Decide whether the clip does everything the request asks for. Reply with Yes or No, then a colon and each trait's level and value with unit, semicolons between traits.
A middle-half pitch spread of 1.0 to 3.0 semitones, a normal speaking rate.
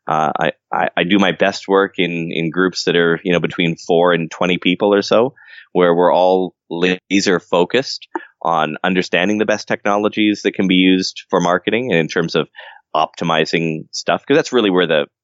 Yes: average, 2.7 semitones; average, 195 wpm